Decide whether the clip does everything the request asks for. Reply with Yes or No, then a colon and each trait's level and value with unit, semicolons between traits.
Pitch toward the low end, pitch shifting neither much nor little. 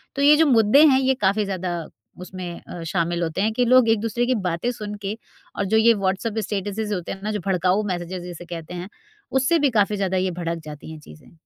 No: high, 200 Hz; average, 4.1 semitones